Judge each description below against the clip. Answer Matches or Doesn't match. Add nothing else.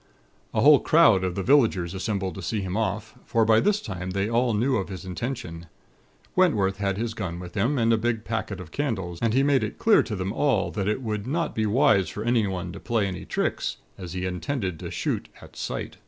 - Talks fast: Matches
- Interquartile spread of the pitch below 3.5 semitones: Doesn't match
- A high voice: Doesn't match